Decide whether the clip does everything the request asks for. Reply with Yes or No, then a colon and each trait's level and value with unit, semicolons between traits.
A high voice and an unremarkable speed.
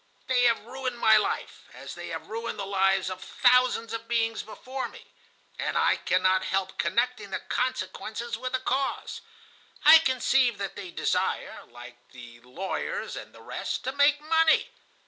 Yes: high, 230 Hz; average, 165 wpm